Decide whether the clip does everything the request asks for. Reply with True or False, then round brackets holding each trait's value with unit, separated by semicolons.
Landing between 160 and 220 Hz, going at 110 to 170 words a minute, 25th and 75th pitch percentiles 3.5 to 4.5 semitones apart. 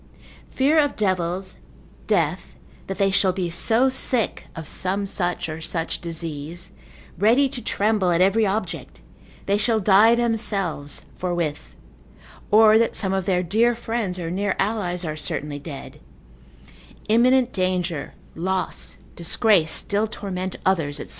True (190 Hz; 135 wpm; 4.0 semitones)